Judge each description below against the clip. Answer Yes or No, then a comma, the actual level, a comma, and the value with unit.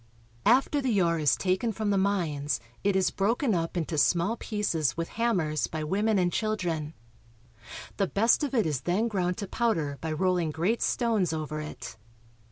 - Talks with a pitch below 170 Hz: No, medium, 185 Hz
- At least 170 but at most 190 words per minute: Yes, average, 175 wpm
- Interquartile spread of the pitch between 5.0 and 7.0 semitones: Yes, average, 5.3 semitones